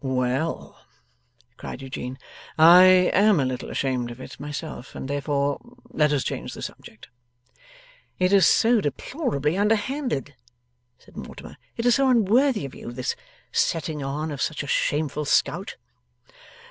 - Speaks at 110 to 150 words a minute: Yes, average, 140 wpm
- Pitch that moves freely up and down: Yes, wide, 6.7 semitones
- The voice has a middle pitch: Yes, medium, 150 Hz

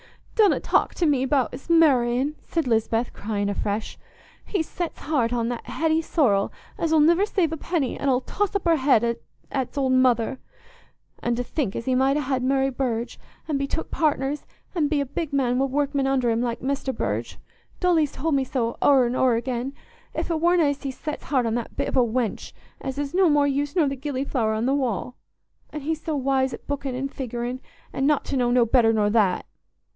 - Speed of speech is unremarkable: No, fast, 210 wpm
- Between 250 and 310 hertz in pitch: Yes, very high, 270 Hz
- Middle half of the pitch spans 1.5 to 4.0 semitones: Yes, average, 3.5 semitones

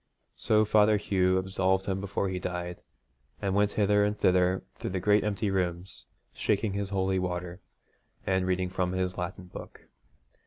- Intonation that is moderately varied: No, narrow, 1.7 semitones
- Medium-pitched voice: No, very low, 95 Hz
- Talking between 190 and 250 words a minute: No, average, 160 wpm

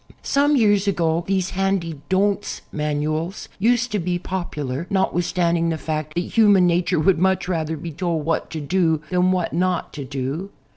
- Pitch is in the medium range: Yes, medium, 175 Hz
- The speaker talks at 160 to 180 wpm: Yes, average, 165 wpm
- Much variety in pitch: No, average, 3.1 semitones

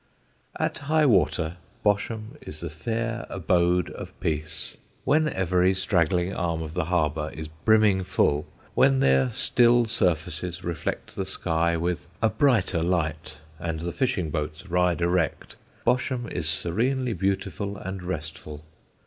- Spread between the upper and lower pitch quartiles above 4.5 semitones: Yes, average, 4.9 semitones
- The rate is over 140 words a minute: No, slow, 135 wpm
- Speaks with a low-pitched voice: Yes, very low, 90 Hz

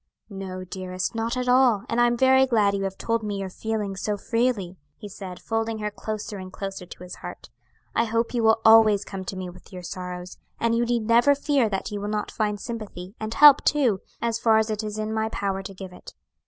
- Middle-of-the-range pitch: No, high, 215 Hz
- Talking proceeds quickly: Yes, fast, 235 wpm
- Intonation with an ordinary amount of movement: Yes, average, 3.1 semitones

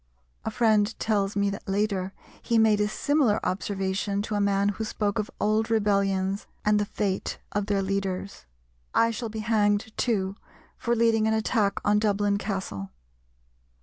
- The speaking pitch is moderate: No, high, 205 Hz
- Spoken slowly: No, average, 160 wpm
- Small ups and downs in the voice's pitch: Yes, narrow, 1.8 semitones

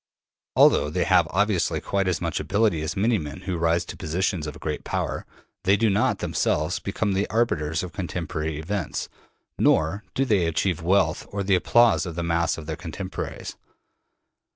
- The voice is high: No, very low, 90 Hz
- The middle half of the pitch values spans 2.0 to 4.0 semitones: Yes, average, 3.6 semitones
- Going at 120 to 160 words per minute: No, average, 175 wpm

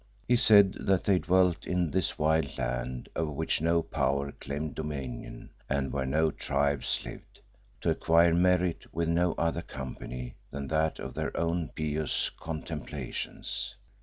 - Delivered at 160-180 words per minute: No, average, 145 wpm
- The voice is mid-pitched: No, very low, 80 Hz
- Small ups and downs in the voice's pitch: No, average, 3.4 semitones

